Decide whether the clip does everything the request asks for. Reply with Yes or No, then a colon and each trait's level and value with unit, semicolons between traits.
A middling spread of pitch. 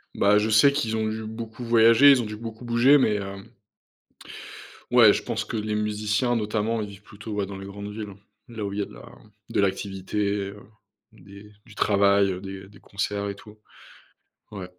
No: narrow, 2.0 semitones